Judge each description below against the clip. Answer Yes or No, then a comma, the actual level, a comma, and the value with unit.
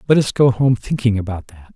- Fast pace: Yes, fast, 240 wpm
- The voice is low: Yes, low, 115 Hz